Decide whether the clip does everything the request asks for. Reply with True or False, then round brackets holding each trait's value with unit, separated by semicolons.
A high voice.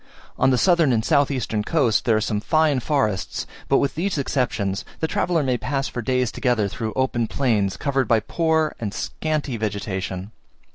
False (125 Hz)